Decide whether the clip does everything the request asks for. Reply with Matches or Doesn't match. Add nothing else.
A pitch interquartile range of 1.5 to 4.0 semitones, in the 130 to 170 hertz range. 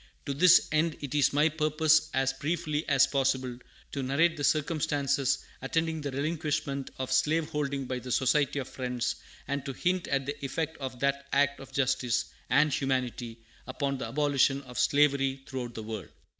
Matches